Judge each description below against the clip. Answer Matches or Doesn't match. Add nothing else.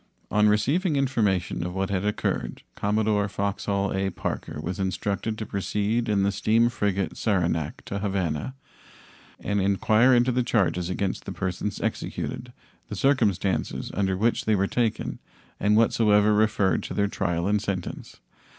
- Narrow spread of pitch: Matches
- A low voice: Matches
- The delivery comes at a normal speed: Matches